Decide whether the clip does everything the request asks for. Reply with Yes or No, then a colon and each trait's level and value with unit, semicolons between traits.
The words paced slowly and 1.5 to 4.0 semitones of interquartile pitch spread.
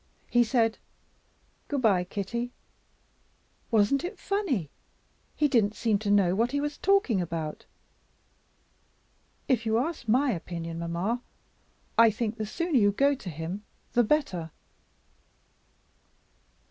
No: slow, 120 wpm; wide, 5.5 semitones